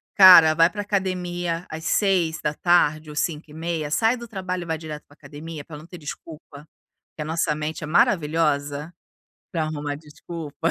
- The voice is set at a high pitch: No, medium, 160 Hz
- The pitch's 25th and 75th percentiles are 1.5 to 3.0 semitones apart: Yes, narrow, 2.6 semitones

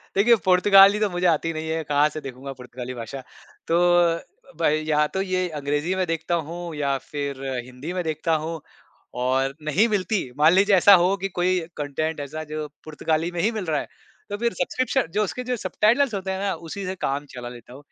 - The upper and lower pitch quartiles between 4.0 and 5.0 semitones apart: Yes, average, 4.7 semitones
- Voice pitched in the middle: Yes, medium, 165 Hz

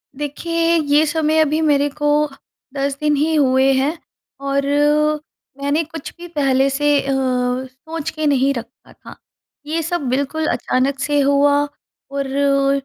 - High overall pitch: Yes, very high, 285 Hz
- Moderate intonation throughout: No, narrow, 2.2 semitones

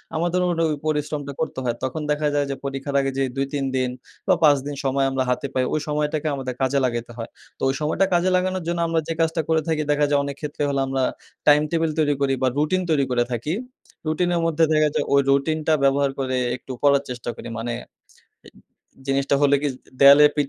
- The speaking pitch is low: No, medium, 145 Hz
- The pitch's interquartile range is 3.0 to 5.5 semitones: No, narrow, 2.4 semitones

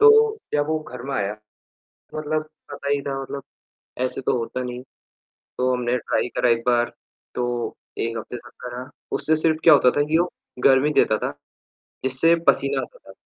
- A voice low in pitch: Yes, low, 130 Hz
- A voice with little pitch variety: No, average, 3.7 semitones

